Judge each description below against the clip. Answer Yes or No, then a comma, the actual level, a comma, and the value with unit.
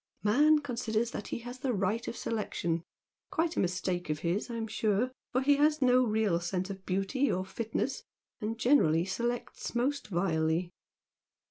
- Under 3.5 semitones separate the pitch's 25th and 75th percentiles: No, average, 5.2 semitones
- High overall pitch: Yes, high, 220 Hz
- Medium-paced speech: Yes, average, 160 wpm